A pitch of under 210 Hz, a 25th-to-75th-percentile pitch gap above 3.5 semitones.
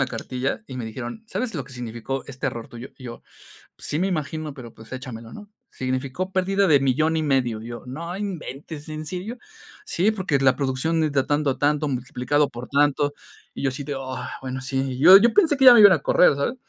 Yes: medium, 140 Hz; average, 4.5 semitones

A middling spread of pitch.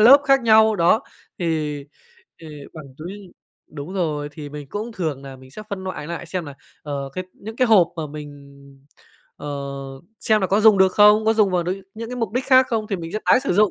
No: wide, 6.1 semitones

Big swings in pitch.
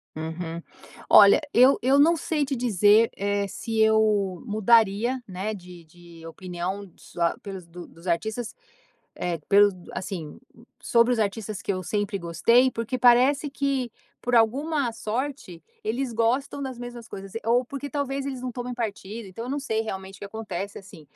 No: average, 4.6 semitones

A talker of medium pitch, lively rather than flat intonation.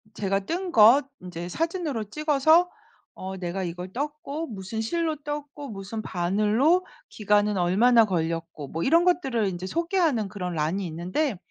No: high, 215 Hz; wide, 8.3 semitones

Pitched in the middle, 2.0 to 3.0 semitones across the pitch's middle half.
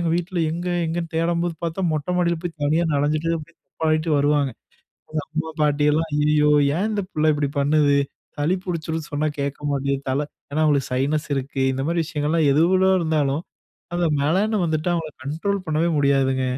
Yes: medium, 155 Hz; average, 2.7 semitones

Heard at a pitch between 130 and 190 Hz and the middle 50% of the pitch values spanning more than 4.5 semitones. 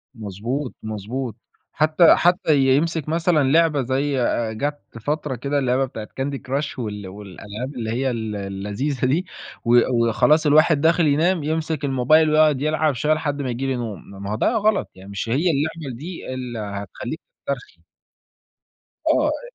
Yes: low, 135 Hz; average, 5.0 semitones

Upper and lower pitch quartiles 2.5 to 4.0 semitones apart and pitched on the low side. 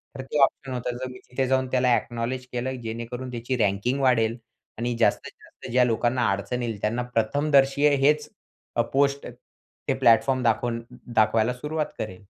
No: narrow, 2.1 semitones; low, 125 Hz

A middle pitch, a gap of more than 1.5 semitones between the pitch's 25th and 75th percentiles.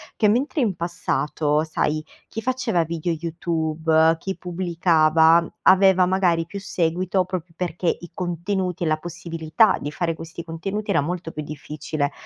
Yes: medium, 170 Hz; narrow, 2.6 semitones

